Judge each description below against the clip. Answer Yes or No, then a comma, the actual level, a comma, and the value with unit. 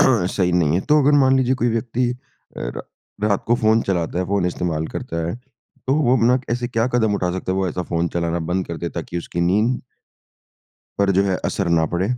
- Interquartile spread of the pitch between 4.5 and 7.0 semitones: Yes, wide, 5.6 semitones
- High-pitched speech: No, low, 100 Hz